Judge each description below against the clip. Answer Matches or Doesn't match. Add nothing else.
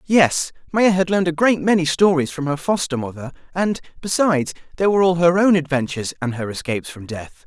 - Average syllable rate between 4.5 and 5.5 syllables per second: Doesn't match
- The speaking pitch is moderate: Matches